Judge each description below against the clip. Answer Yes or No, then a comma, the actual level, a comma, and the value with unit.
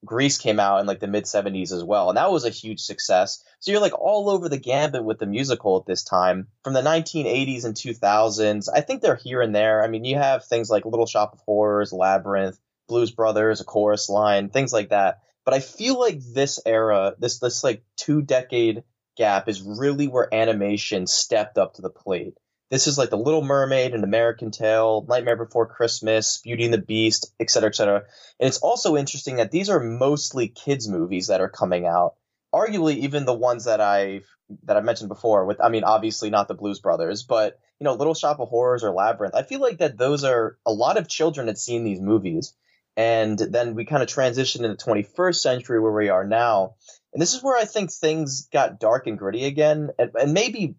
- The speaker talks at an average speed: No, fast, 220 wpm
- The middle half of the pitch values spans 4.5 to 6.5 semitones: Yes, average, 4.8 semitones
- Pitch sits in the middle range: No, low, 115 Hz